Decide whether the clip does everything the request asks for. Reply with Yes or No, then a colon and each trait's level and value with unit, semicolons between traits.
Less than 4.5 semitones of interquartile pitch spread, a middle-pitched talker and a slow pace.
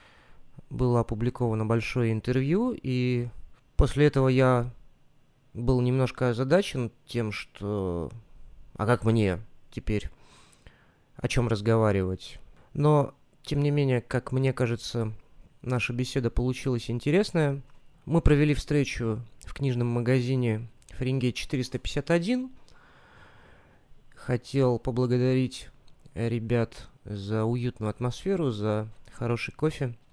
No: average, 2.7 semitones; low, 125 Hz; slow, 95 wpm